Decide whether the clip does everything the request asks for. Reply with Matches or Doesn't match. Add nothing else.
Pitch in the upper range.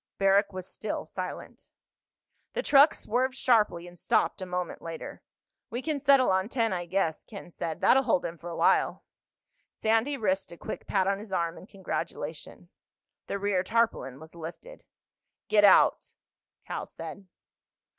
Matches